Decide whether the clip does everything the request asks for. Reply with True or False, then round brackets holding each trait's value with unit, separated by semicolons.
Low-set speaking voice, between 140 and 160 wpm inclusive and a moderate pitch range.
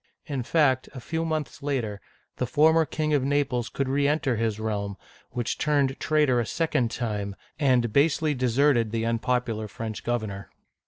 True (125 Hz; 155 wpm; 4.2 semitones)